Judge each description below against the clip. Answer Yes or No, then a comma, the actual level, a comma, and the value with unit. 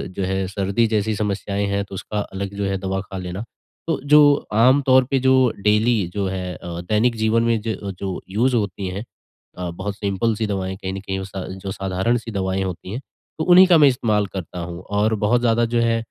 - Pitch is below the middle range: Yes, low, 100 Hz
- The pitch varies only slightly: No, average, 3.2 semitones